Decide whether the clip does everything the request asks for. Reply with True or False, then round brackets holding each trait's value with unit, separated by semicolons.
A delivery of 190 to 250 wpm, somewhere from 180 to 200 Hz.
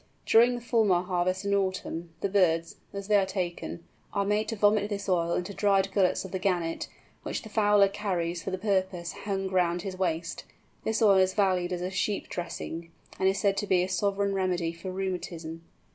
True (200 wpm; 190 Hz)